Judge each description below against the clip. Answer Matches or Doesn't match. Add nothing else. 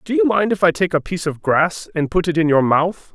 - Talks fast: Matches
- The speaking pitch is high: Doesn't match